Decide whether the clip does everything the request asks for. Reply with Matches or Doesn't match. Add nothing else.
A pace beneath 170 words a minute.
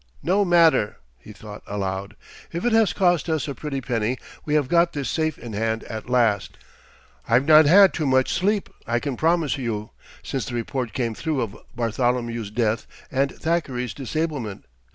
Doesn't match